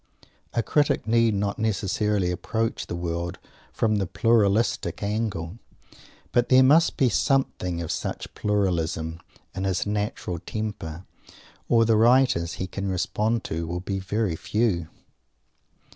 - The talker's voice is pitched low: Yes, low, 105 Hz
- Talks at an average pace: No, slow, 130 wpm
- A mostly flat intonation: No, average, 4.3 semitones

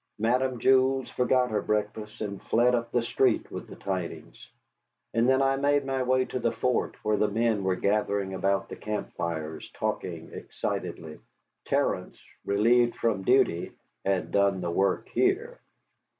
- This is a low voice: Yes, low, 115 Hz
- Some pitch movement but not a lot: Yes, average, 4.5 semitones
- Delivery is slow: No, average, 155 wpm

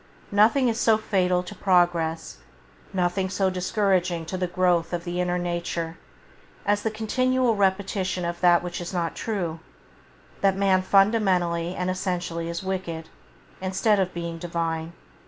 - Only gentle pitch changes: Yes, narrow, 2.3 semitones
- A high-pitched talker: No, medium, 180 Hz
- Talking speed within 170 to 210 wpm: No, average, 145 wpm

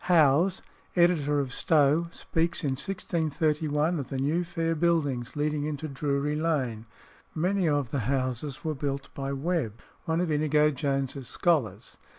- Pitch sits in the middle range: Yes, medium, 150 Hz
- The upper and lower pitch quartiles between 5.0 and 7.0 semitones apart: No, average, 3.2 semitones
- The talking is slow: No, average, 145 wpm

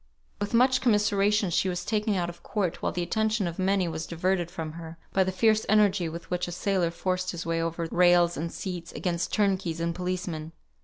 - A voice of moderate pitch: Yes, medium, 180 Hz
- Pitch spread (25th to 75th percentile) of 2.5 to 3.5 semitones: Yes, average, 2.9 semitones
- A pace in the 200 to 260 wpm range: Yes, fast, 205 wpm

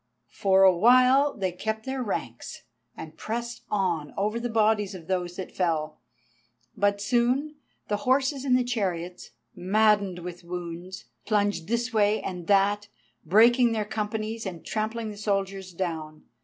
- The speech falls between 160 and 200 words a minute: No, average, 140 wpm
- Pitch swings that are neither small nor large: Yes, average, 4.1 semitones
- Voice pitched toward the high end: Yes, high, 205 Hz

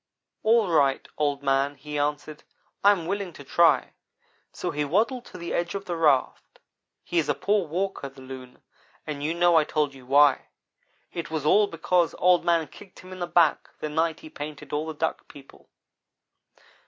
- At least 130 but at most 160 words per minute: No, average, 190 wpm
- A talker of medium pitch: Yes, medium, 160 Hz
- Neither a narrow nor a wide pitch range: Yes, average, 3.3 semitones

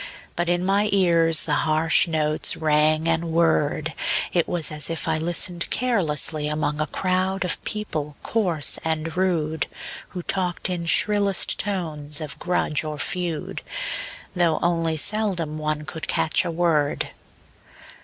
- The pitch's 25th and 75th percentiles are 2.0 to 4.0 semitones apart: Yes, average, 2.7 semitones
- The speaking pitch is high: No, medium, 165 Hz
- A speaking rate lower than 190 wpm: Yes, average, 140 wpm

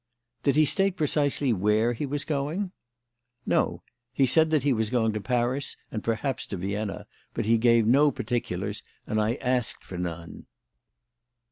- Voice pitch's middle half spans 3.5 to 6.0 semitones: Yes, average, 4.8 semitones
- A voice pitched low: Yes, low, 125 Hz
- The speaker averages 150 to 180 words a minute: Yes, average, 160 wpm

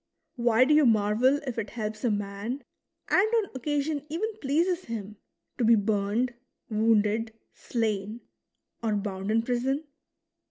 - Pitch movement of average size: Yes, average, 4.2 semitones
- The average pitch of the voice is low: No, high, 230 Hz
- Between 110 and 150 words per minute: Yes, slow, 135 wpm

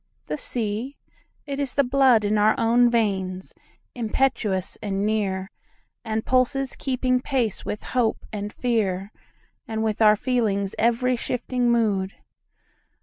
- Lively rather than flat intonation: No, average, 3.4 semitones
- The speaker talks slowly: Yes, slow, 115 wpm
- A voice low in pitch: No, high, 225 Hz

